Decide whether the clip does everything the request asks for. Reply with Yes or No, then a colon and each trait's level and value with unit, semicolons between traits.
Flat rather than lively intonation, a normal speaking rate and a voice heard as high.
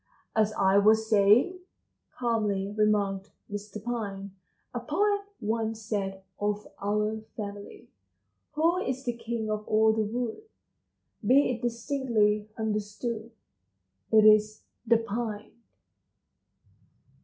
No: narrow, 2.3 semitones; slow, 110 wpm; high, 215 Hz